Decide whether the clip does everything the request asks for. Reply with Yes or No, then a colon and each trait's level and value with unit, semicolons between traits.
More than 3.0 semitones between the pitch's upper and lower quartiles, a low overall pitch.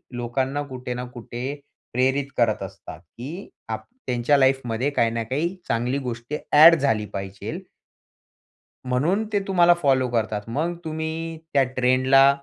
Yes: average, 3.7 semitones; low, 130 Hz